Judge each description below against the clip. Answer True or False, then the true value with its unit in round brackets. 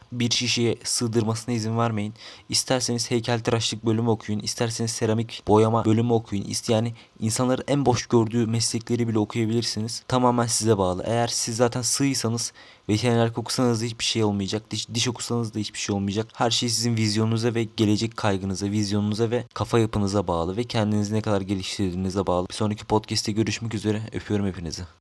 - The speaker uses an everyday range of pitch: False (2.1 semitones)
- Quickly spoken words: True (165 wpm)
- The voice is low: True (115 Hz)